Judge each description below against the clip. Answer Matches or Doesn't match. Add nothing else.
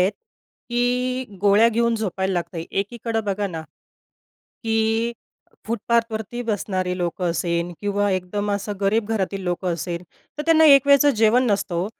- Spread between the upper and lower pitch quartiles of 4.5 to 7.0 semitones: Doesn't match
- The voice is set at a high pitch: Matches